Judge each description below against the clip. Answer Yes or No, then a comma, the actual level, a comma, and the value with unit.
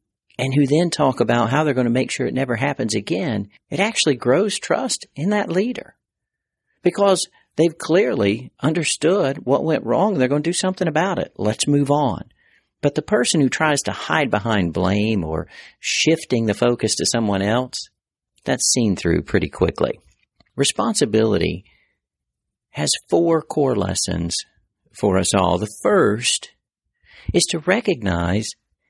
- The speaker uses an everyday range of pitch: No, wide, 7.8 semitones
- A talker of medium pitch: No, low, 130 Hz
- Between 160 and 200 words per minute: No, average, 150 wpm